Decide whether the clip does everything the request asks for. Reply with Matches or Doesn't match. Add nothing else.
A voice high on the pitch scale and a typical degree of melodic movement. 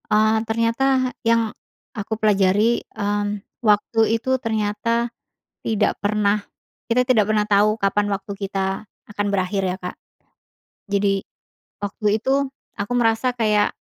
Doesn't match